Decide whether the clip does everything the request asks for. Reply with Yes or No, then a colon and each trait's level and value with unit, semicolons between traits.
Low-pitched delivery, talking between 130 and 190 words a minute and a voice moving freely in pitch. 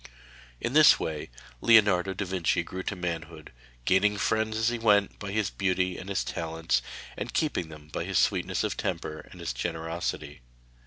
No: very low, 95 Hz; average, 170 wpm; average, 4.1 semitones